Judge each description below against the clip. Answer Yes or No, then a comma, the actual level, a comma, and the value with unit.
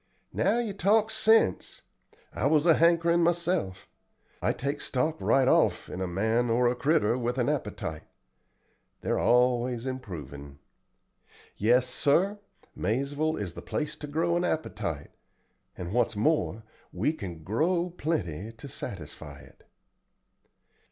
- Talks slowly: Yes, slow, 130 wpm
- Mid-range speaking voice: No, low, 125 Hz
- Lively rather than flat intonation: Yes, wide, 7.8 semitones